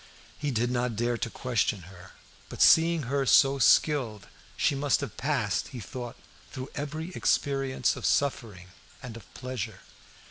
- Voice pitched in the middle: No, low, 130 Hz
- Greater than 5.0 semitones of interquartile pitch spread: No, average, 3.4 semitones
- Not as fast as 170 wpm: Yes, average, 150 wpm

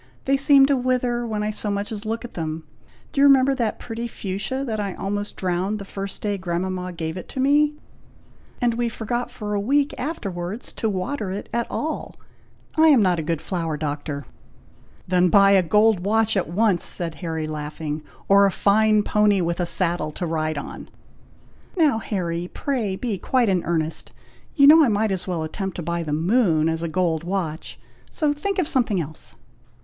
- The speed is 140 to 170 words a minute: No, average, 190 wpm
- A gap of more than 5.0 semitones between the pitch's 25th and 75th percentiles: Yes, wide, 5.6 semitones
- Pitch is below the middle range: No, high, 200 Hz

